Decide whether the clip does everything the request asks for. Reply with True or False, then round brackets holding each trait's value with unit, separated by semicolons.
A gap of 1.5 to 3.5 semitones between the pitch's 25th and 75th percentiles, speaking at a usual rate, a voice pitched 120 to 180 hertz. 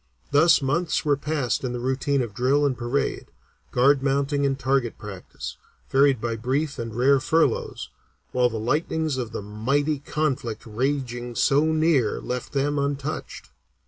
True (2.9 semitones; 150 wpm; 135 Hz)